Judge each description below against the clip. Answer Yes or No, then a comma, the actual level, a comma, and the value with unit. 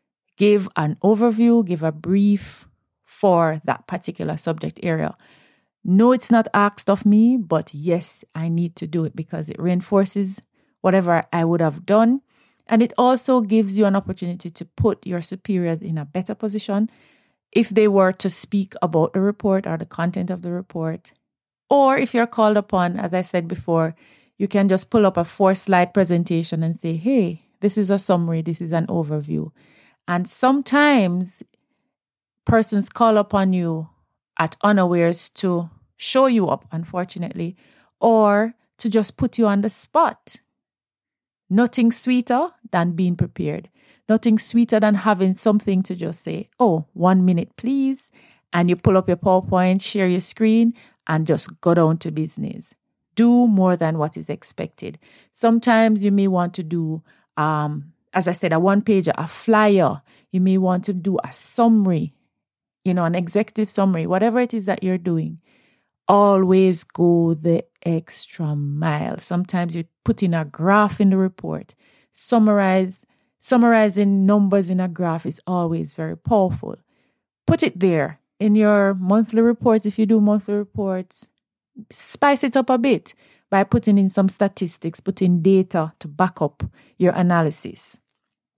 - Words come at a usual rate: Yes, average, 160 wpm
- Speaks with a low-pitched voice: No, high, 190 Hz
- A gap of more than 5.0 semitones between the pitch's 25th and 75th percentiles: No, average, 4.0 semitones